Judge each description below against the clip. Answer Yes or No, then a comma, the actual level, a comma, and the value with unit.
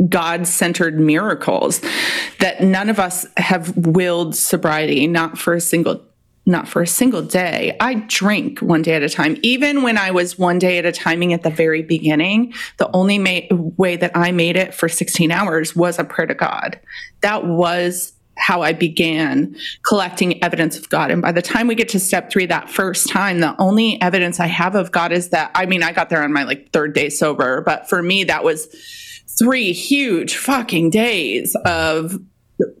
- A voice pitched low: No, medium, 180 Hz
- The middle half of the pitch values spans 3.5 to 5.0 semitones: No, average, 2.8 semitones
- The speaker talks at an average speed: Yes, average, 190 wpm